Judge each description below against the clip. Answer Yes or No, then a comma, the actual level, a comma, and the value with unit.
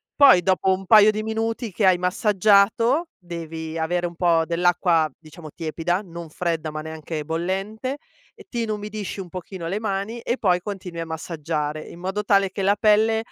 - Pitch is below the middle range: No, medium, 185 Hz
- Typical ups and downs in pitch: Yes, average, 4.1 semitones